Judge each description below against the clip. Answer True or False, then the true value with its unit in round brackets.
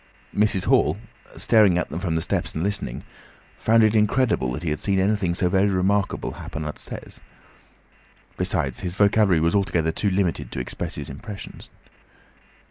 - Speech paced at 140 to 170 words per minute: True (160 wpm)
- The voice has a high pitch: False (95 Hz)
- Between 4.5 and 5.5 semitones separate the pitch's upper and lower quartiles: False (3.9 semitones)